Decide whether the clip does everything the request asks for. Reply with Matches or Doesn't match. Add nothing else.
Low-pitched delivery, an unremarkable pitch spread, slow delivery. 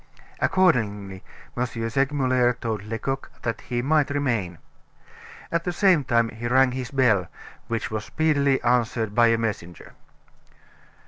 Matches